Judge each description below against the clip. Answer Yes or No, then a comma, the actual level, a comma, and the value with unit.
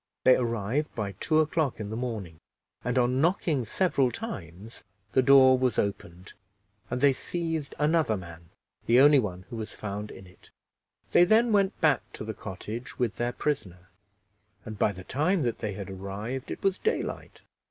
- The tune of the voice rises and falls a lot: Yes, wide, 6.6 semitones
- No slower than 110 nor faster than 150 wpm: No, average, 175 wpm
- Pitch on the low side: Yes, low, 120 Hz